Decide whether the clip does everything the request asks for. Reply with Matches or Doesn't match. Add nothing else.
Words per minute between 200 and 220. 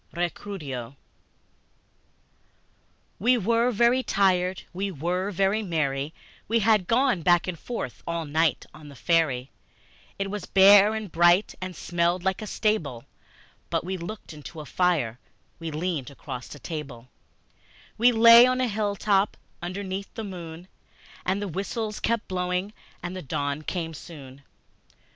Doesn't match